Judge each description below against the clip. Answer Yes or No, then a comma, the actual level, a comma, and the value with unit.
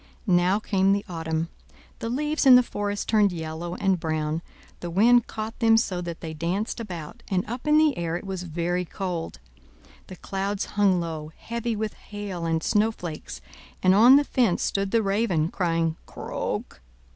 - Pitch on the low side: No, high, 190 Hz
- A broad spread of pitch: No, average, 4.5 semitones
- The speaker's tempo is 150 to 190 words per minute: Yes, average, 170 wpm